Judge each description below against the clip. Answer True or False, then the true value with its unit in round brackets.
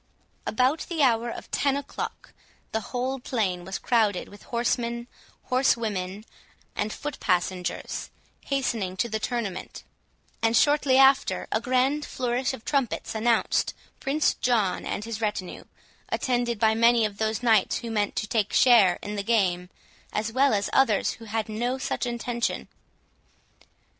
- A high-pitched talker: True (230 Hz)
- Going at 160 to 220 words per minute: False (145 wpm)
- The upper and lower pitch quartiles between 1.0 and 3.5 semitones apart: True (3.2 semitones)